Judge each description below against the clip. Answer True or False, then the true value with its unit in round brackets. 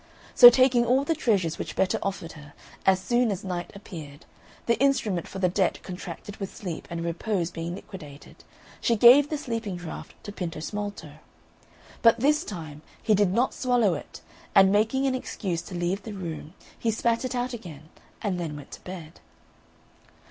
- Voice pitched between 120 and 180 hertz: False (195 Hz)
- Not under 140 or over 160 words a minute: False (175 wpm)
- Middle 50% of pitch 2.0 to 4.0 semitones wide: False (5.5 semitones)